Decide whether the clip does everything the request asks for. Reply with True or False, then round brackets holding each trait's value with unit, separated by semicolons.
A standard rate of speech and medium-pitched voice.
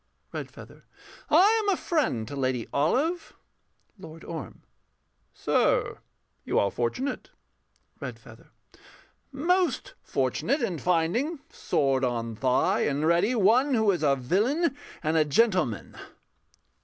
False (115 wpm; 175 Hz)